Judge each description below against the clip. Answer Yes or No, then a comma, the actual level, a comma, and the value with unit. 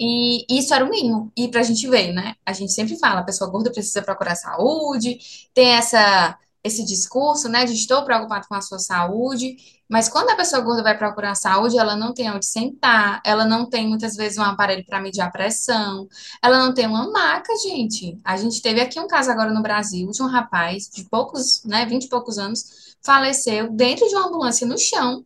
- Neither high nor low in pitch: No, high, 230 Hz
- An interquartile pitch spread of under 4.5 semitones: Yes, average, 3.5 semitones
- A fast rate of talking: Yes, fast, 220 wpm